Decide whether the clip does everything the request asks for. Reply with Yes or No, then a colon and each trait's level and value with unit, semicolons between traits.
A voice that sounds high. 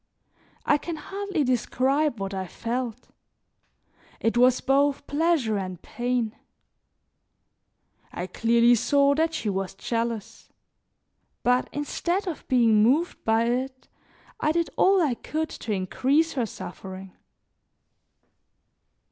Yes: very high, 250 Hz